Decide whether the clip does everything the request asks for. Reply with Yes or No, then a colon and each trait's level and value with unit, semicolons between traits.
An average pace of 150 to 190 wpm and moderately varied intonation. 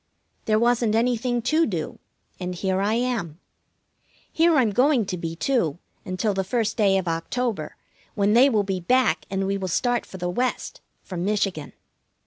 Yes: average, 170 wpm; average, 4.7 semitones